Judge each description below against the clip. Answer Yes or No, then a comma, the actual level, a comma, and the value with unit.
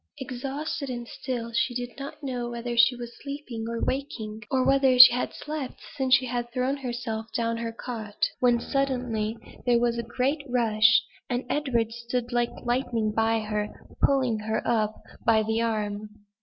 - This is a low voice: No, high, 240 Hz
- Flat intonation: Yes, narrow, 2.2 semitones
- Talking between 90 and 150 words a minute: No, average, 175 wpm